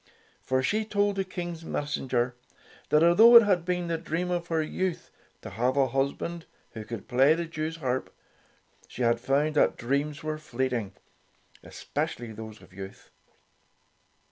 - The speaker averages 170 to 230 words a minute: No, average, 160 wpm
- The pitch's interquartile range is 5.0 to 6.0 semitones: Yes, wide, 5.5 semitones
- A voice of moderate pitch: Yes, medium, 150 Hz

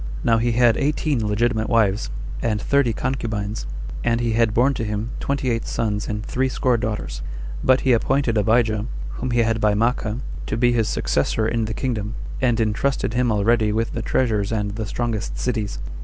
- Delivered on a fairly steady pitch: Yes, narrow, 2.2 semitones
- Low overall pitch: Yes, low, 115 Hz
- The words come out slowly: No, average, 180 wpm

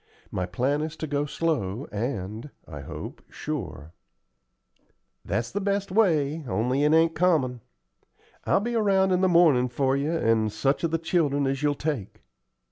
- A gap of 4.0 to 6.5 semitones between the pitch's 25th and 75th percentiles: Yes, wide, 5.6 semitones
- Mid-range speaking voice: Yes, medium, 145 Hz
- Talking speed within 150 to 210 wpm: Yes, average, 160 wpm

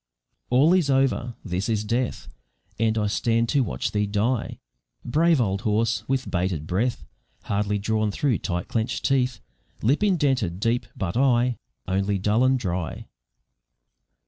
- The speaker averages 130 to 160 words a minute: Yes, average, 145 wpm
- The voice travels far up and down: No, average, 4.1 semitones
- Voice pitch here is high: No, low, 115 Hz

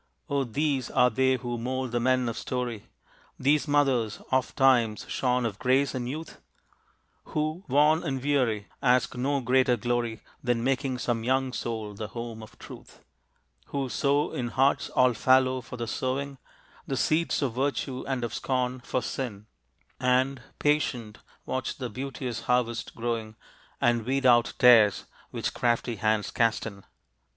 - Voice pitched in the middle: No, low, 125 Hz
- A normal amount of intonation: No, narrow, 2.3 semitones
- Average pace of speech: Yes, average, 150 wpm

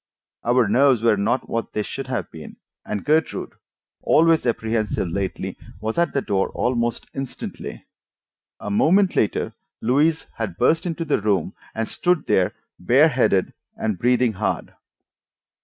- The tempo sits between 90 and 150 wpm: Yes, average, 140 wpm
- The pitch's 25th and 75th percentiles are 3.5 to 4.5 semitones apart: No, average, 5.1 semitones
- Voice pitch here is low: Yes, low, 120 Hz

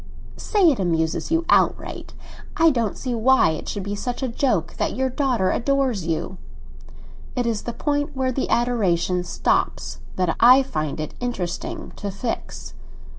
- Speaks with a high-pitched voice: Yes, high, 235 Hz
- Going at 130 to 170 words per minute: Yes, average, 160 wpm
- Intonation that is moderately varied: No, wide, 6.4 semitones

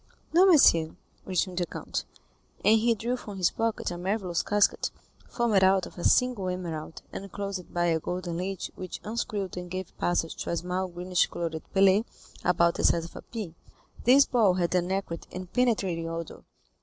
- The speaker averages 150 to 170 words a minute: No, average, 180 wpm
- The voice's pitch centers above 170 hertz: Yes, medium, 185 Hz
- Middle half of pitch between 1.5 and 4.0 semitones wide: Yes, average, 3.1 semitones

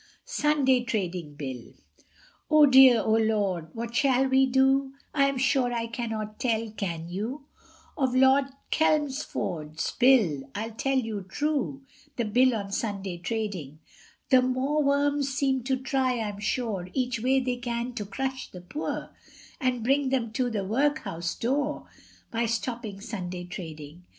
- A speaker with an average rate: Yes, average, 145 wpm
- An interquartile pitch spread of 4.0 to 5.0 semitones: Yes, average, 4.7 semitones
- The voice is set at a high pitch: Yes, high, 240 Hz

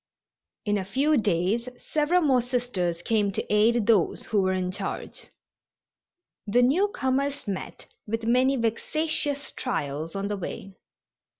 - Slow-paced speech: Yes, slow, 130 wpm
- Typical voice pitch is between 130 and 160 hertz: No, high, 230 Hz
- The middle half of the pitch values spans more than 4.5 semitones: Yes, average, 5.3 semitones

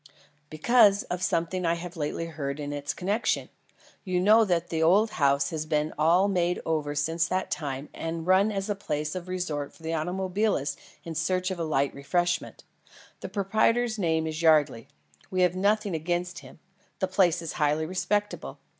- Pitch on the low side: No, medium, 170 Hz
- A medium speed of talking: Yes, average, 170 wpm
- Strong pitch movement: No, average, 3.4 semitones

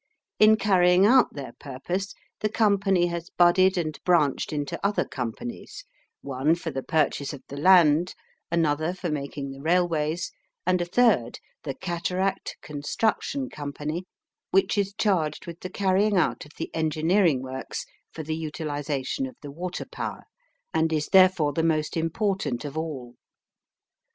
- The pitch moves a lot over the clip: No, average, 4.3 semitones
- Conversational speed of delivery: Yes, average, 145 wpm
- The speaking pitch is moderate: Yes, medium, 165 Hz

